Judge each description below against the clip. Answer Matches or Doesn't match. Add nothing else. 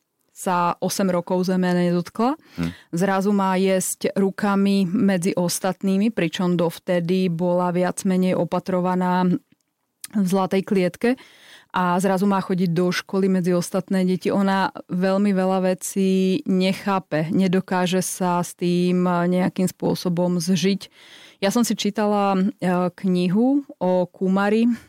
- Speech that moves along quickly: Doesn't match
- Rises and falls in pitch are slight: Matches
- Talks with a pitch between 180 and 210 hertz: Matches